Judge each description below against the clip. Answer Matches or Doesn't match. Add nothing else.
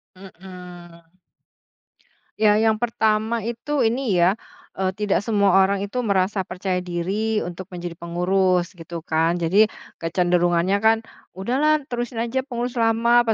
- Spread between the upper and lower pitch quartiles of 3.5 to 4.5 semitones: Matches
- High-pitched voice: Matches